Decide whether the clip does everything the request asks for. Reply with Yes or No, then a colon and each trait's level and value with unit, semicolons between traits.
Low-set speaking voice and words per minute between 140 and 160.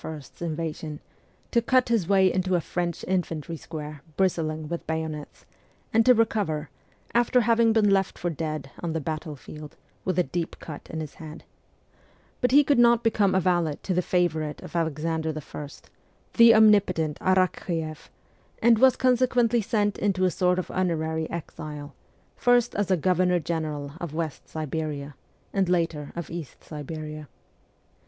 No: medium, 170 Hz; average, 155 wpm